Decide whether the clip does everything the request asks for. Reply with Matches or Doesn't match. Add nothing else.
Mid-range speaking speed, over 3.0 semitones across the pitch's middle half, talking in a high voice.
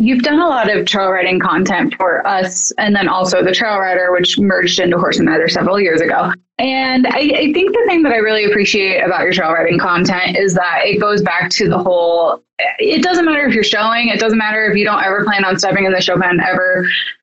Doesn't match